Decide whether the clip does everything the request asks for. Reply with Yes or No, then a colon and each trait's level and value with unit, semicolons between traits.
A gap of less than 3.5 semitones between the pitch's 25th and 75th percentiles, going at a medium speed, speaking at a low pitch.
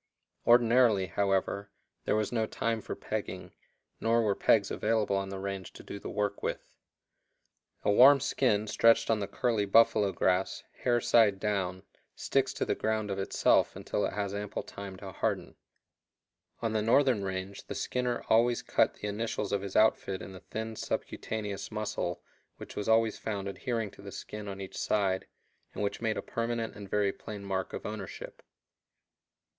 Yes: narrow, 2.5 semitones; average, 170 wpm; low, 105 Hz